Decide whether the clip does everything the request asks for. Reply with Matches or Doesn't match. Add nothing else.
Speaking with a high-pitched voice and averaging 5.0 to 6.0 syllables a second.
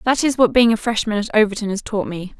Doesn't match